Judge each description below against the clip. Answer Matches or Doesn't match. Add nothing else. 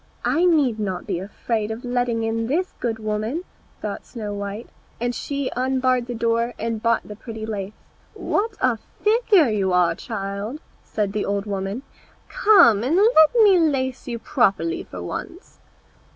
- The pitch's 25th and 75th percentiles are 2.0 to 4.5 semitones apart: Doesn't match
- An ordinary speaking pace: Matches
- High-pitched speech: Matches